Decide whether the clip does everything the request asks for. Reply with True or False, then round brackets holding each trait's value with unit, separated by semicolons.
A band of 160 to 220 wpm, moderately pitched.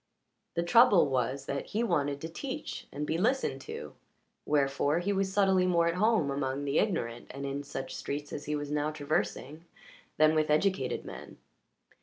True (175 wpm; 155 Hz)